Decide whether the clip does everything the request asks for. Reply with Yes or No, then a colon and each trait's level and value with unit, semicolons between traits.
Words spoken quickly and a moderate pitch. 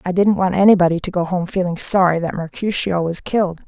Yes: fast, 210 wpm; medium, 180 Hz